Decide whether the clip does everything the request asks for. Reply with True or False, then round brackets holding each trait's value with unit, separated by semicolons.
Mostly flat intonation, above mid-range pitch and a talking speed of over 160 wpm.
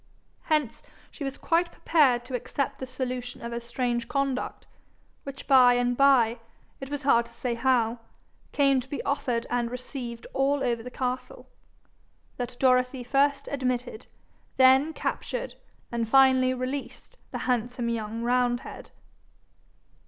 False (2.2 semitones; 255 Hz; 135 wpm)